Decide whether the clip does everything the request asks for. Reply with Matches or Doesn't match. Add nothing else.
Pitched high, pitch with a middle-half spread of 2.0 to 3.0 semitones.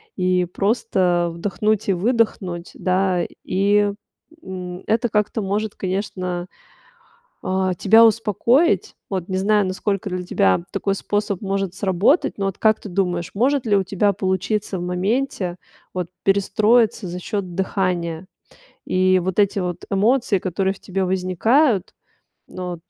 Matches